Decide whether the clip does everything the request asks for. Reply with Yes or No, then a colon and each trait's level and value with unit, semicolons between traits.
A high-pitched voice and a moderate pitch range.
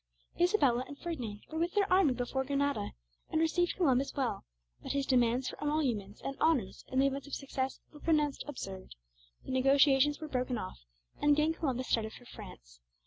Yes: very high, 275 Hz; average, 3.5 semitones